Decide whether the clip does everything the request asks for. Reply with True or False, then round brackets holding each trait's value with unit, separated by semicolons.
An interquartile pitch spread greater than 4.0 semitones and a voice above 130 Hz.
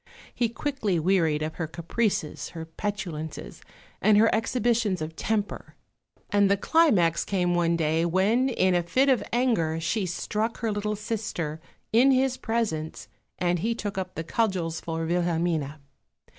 True (5.4 semitones; 190 Hz)